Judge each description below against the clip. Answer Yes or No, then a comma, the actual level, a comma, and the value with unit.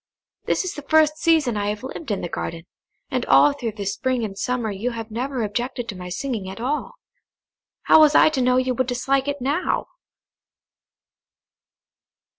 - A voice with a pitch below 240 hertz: No, very high, 250 Hz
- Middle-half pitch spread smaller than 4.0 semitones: No, average, 4.6 semitones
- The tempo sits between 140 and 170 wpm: No, average, 180 wpm